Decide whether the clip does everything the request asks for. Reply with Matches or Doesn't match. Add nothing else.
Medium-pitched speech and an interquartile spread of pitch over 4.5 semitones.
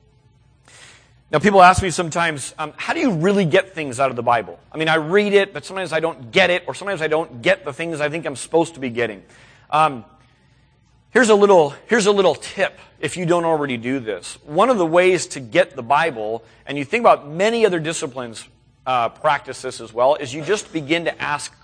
Matches